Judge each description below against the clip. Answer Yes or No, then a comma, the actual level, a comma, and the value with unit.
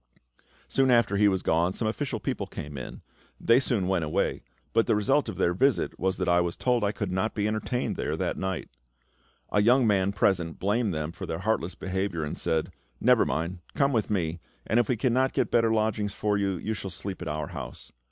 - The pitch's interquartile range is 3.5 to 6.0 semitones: Yes, average, 4.2 semitones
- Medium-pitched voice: No, low, 100 Hz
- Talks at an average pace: No, fast, 215 wpm